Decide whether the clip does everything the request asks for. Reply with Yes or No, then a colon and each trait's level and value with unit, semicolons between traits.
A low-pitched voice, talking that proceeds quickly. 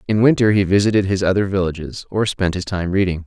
Yes: very low, 95 Hz; fast, 220 wpm